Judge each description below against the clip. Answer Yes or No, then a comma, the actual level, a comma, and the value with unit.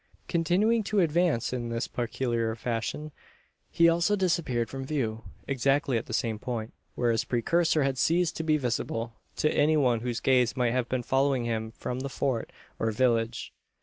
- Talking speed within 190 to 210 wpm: No, average, 175 wpm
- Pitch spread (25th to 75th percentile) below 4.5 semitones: No, average, 4.9 semitones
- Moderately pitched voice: No, low, 130 Hz